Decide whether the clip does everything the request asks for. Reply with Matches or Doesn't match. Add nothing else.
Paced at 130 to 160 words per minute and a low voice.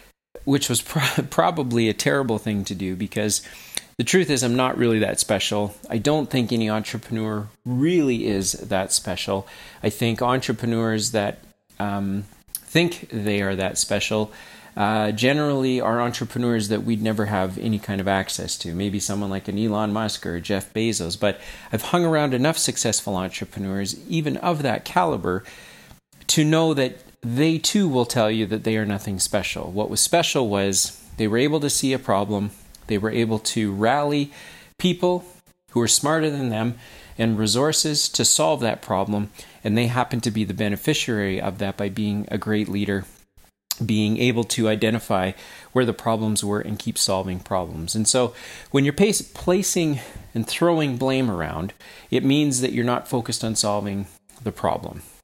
Doesn't match